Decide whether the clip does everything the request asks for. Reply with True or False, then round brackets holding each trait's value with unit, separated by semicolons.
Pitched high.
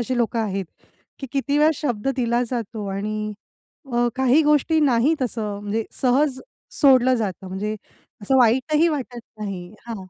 True (240 Hz)